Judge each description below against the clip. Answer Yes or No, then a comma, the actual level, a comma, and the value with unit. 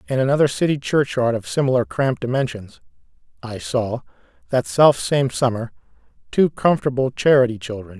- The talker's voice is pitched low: Yes, low, 130 Hz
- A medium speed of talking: No, slow, 130 wpm